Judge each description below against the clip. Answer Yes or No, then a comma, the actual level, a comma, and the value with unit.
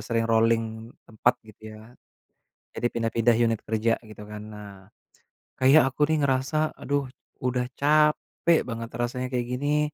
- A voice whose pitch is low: Yes, low, 120 Hz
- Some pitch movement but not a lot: Yes, average, 3.7 semitones